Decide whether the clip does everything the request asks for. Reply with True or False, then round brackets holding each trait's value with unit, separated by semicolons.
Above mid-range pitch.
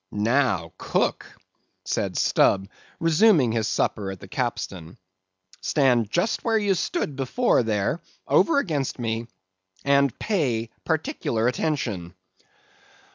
False (125 Hz)